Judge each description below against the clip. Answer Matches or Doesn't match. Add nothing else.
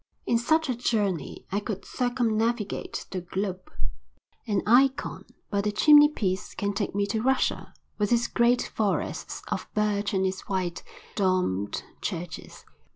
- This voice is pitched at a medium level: Doesn't match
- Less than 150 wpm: Matches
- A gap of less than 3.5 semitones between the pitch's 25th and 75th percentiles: Doesn't match